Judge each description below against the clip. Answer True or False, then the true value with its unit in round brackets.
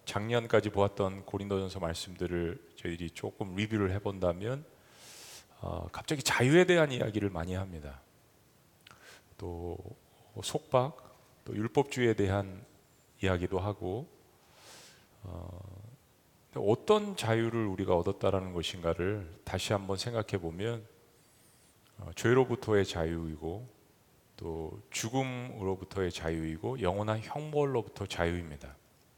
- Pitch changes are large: False (4.4 semitones)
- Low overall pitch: True (100 Hz)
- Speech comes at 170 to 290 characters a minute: True (260 characters per minute)